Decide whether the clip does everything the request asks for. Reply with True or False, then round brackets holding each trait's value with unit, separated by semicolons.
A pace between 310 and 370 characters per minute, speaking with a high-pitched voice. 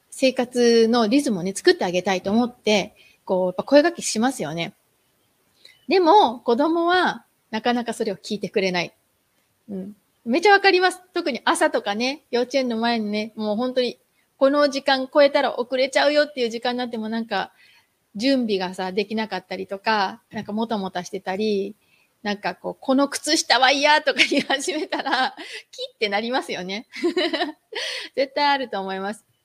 True (345 characters per minute; 240 Hz)